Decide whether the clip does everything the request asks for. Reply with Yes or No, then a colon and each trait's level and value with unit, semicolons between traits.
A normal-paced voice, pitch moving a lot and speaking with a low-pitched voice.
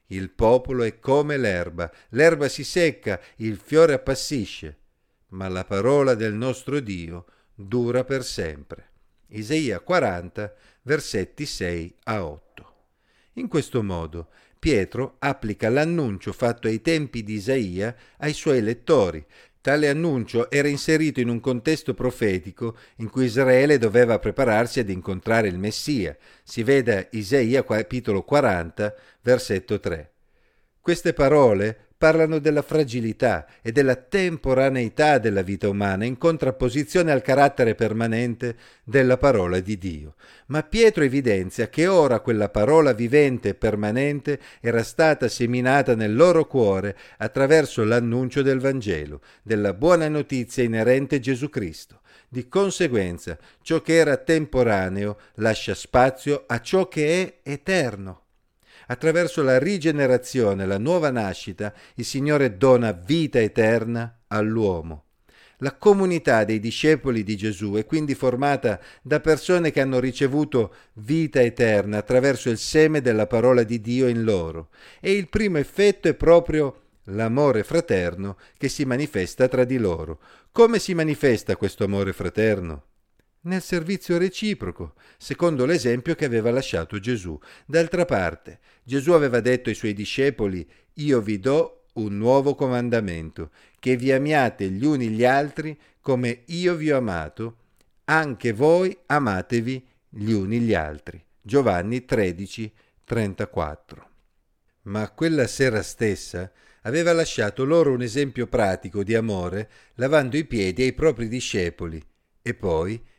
Yes: average, 130 wpm; wide, 5.7 semitones; low, 125 Hz